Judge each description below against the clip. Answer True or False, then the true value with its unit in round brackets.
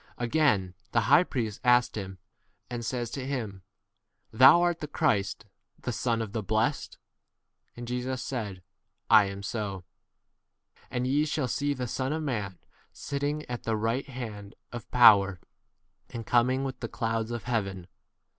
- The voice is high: False (120 Hz)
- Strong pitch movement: False (3.7 semitones)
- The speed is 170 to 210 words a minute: False (160 wpm)